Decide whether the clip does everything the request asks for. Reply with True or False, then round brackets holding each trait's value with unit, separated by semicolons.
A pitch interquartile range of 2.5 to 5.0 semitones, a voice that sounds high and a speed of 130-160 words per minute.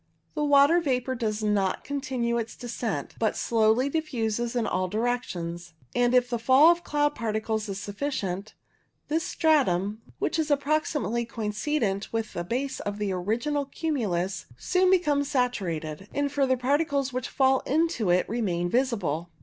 False (5.5 semitones; 240 Hz; 150 wpm)